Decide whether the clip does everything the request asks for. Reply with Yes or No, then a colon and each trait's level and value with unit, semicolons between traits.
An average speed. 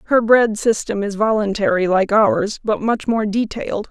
Yes: average, 170 wpm